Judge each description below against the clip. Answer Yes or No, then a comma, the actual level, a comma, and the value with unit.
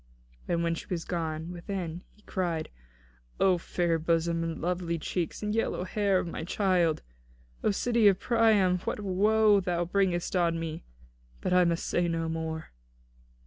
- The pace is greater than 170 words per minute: No, average, 165 wpm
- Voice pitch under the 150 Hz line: No, medium, 175 Hz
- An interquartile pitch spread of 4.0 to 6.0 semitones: No, average, 2.7 semitones